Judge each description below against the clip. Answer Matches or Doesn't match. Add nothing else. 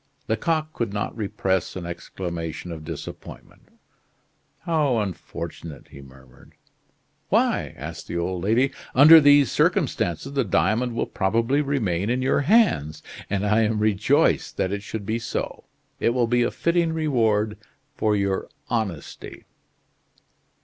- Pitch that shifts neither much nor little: Doesn't match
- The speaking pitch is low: Matches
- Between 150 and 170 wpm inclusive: Doesn't match